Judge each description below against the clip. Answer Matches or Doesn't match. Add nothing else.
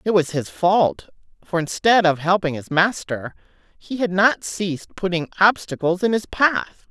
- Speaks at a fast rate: Doesn't match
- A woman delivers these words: Matches